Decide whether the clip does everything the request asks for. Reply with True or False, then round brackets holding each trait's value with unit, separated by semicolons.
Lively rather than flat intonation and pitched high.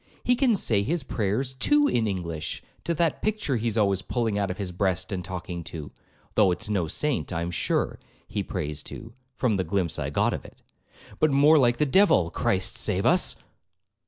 False (7.1 semitones; 105 Hz)